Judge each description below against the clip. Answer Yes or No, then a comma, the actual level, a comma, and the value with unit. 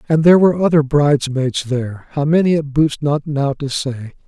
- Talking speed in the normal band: Yes, average, 195 wpm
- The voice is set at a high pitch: No, medium, 145 Hz